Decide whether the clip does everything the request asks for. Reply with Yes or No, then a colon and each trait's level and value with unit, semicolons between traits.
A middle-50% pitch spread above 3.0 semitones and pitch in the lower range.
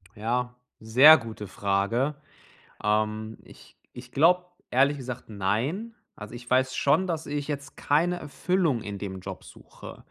Yes: wide, 5.4 semitones; low, 125 Hz